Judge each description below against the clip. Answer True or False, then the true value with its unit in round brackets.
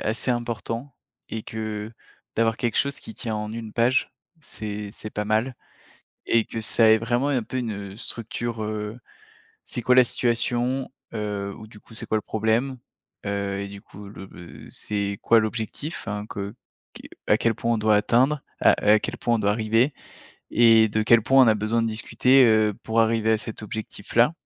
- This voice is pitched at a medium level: False (110 Hz)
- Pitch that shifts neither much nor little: False (2.0 semitones)